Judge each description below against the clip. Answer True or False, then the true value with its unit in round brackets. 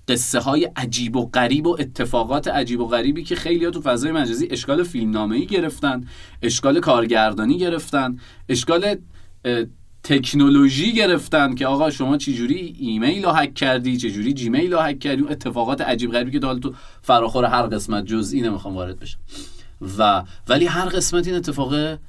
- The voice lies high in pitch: False (135 Hz)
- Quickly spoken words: True (160 wpm)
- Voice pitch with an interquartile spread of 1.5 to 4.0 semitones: False (5.2 semitones)